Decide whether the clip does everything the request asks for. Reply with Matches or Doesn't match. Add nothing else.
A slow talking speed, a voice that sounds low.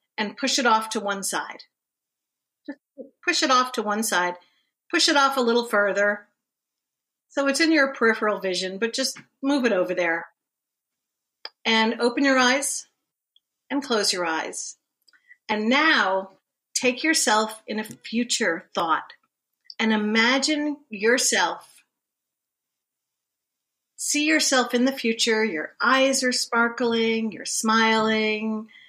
Doesn't match